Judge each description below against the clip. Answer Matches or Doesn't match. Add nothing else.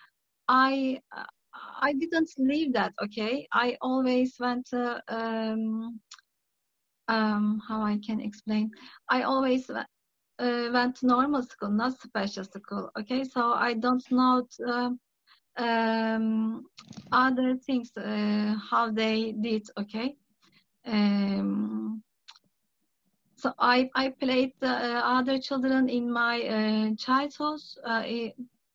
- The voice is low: Doesn't match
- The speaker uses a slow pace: Matches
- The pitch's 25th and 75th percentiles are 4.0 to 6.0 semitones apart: Doesn't match